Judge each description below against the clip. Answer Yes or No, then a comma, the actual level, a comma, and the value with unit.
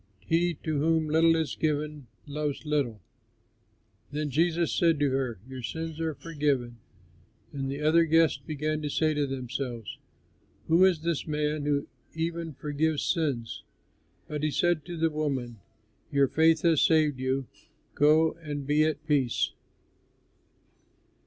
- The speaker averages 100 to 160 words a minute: Yes, average, 140 wpm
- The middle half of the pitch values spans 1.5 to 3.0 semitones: Yes, narrow, 2.5 semitones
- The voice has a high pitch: No, medium, 150 Hz